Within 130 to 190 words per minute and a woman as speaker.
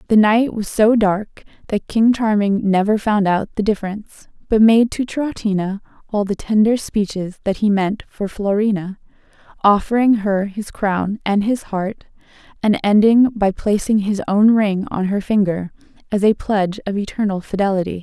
Yes: average, 165 wpm; female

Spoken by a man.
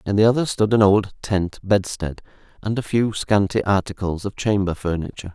Yes: male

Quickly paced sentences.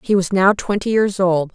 Yes: fast, 235 wpm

